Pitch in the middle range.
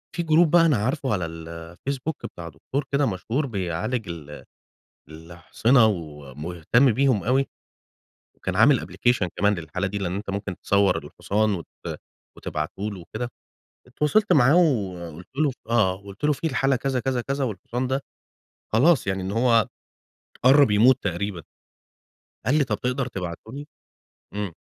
No: low, 110 Hz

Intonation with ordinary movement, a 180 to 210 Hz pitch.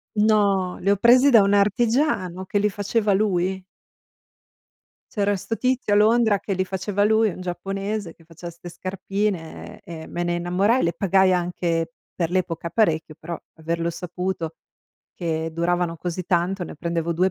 Yes: average, 3.1 semitones; medium, 185 Hz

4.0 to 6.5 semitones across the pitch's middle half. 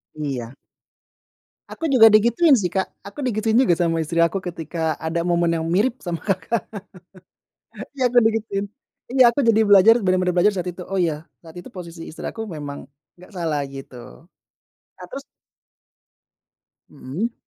Yes: average, 5.1 semitones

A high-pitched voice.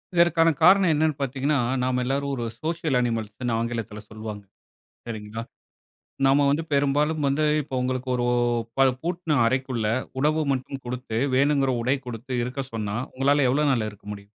No: low, 135 Hz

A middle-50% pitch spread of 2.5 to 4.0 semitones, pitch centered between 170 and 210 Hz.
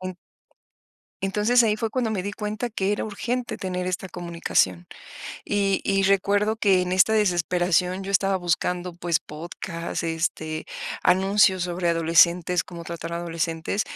Yes: average, 2.9 semitones; medium, 185 Hz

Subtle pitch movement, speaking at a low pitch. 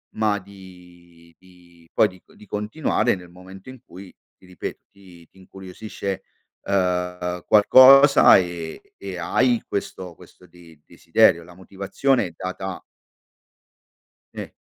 Yes: narrow, 2.2 semitones; very low, 95 Hz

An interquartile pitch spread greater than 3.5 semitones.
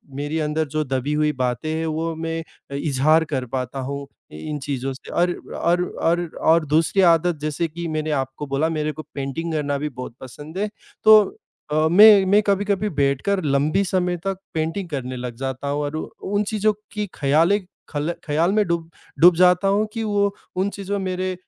Yes: average, 4.5 semitones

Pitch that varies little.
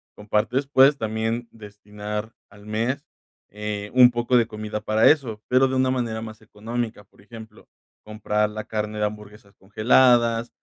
Yes: narrow, 2.2 semitones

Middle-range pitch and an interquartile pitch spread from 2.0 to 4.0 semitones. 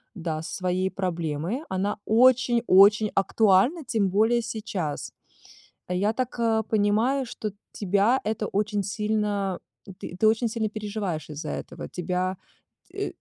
No: high, 205 Hz; average, 3.2 semitones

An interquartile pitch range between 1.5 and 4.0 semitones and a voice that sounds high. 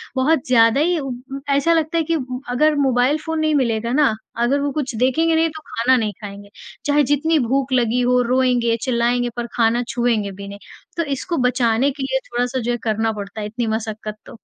Yes: average, 3.7 semitones; very high, 250 Hz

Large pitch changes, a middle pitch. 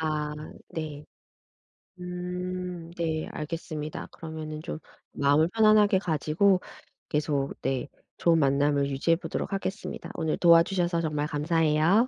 No: average, 2.9 semitones; medium, 160 Hz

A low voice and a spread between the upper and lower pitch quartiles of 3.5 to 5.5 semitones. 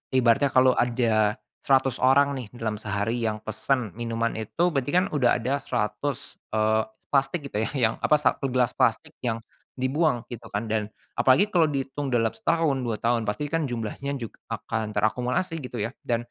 Yes: low, 125 Hz; average, 3.8 semitones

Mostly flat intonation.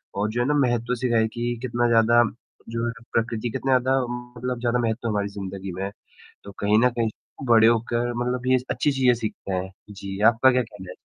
Yes: narrow, 2.2 semitones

